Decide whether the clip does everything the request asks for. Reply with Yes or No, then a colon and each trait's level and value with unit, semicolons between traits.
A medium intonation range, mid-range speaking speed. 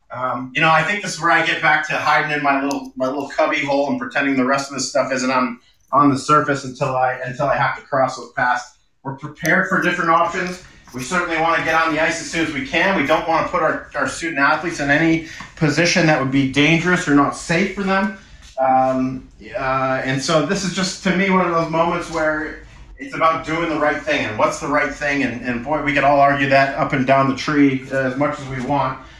No: average, 3.4 semitones; fast, 255 wpm